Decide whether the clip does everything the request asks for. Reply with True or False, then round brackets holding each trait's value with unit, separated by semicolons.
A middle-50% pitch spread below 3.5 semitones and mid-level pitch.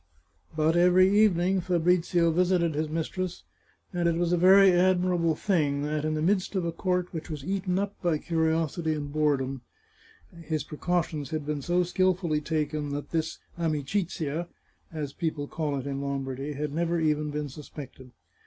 True (3.0 semitones; 160 Hz)